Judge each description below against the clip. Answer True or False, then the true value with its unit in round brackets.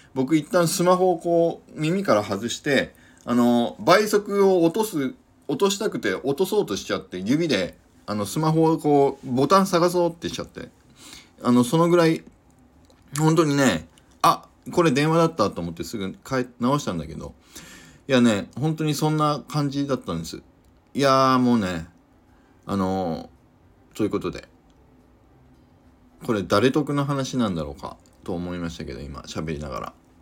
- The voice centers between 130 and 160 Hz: True (140 Hz)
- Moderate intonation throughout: False (8.2 semitones)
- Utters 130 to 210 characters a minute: False (300 characters per minute)